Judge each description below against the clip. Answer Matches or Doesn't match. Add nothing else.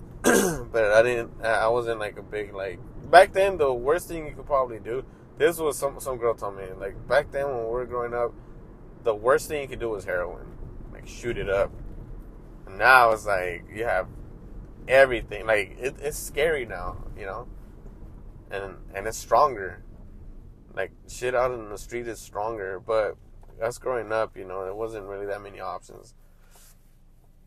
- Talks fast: Doesn't match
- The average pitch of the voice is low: Matches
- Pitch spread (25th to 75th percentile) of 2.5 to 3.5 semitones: Doesn't match